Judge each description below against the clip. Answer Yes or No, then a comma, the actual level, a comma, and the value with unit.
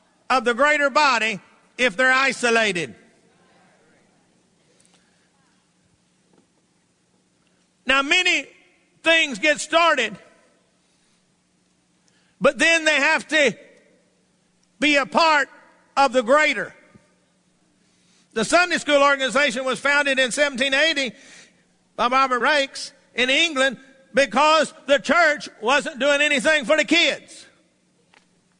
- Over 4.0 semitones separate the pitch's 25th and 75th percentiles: No, average, 2.7 semitones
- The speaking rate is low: Yes, slow, 95 wpm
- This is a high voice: Yes, very high, 280 Hz